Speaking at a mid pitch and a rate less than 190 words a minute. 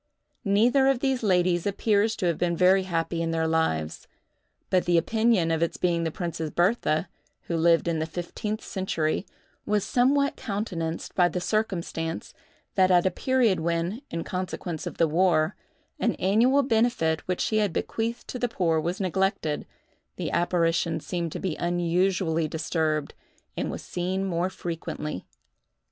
Yes: medium, 175 Hz; average, 155 wpm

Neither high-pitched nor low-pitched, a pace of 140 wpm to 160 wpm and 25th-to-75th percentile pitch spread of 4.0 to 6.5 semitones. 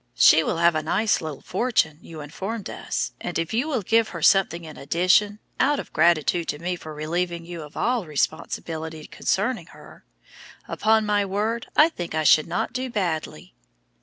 No: medium, 175 Hz; average, 180 wpm; average, 5.2 semitones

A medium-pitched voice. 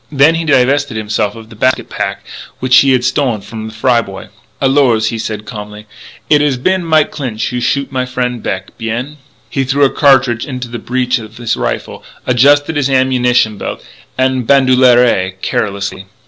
No: low, 125 Hz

